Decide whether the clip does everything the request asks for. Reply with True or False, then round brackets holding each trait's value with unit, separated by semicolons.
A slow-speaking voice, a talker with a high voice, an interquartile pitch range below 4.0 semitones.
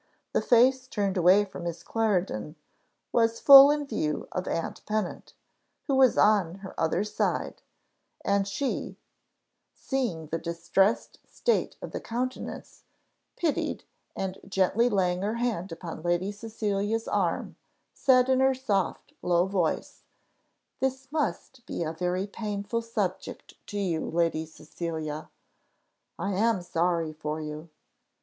False (130 wpm; 195 Hz; 5.2 semitones)